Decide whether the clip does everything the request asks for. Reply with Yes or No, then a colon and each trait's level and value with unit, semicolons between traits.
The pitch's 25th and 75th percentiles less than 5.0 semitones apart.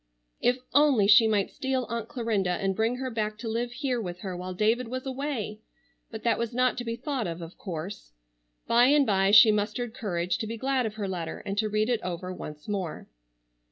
Yes: average, 4.1 semitones